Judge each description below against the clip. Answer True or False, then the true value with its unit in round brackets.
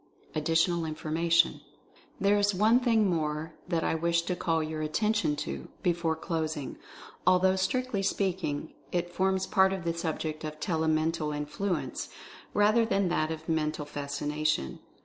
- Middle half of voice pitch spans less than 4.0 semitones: True (3.5 semitones)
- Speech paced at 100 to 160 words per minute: True (150 wpm)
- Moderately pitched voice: True (165 Hz)